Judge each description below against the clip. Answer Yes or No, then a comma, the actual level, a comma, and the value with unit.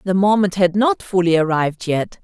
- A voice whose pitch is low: No, medium, 185 Hz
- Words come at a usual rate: Yes, average, 190 wpm